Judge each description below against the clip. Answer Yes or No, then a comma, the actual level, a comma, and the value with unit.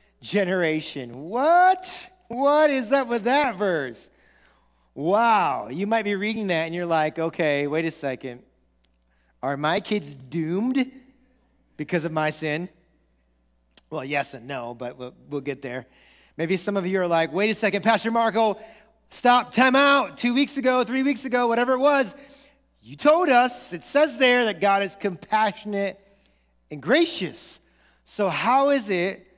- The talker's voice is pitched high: Yes, high, 200 Hz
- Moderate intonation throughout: No, wide, 8.7 semitones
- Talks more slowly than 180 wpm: Yes, average, 155 wpm